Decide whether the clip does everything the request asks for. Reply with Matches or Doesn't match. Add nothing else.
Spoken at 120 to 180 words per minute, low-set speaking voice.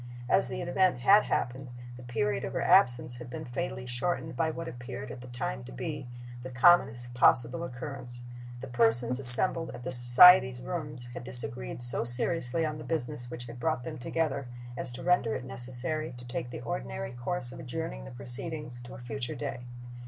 Doesn't match